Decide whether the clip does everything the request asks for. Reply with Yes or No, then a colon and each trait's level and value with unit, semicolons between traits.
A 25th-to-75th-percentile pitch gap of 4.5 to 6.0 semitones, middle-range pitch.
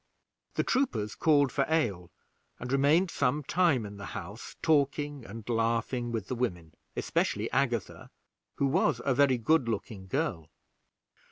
No: average, 5.1 semitones; low, 125 Hz